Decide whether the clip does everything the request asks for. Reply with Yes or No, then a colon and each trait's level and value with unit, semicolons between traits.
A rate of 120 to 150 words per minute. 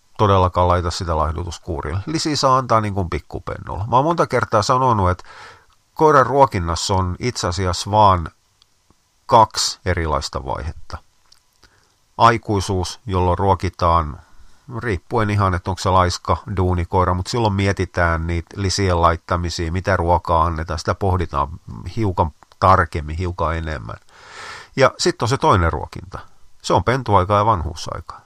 Yes: average, 125 wpm